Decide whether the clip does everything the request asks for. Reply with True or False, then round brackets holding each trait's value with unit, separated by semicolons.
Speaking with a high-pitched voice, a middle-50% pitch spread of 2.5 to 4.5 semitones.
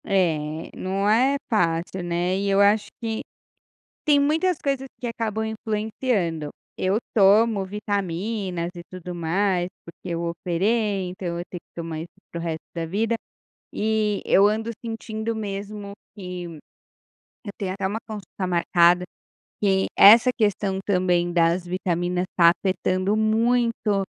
True (195 Hz; 3.7 semitones)